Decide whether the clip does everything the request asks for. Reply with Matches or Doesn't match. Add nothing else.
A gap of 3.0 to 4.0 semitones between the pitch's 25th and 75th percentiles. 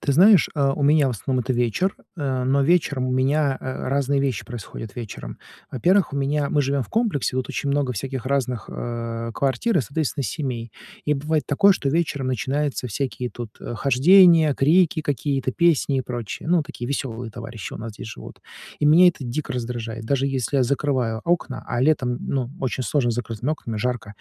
Matches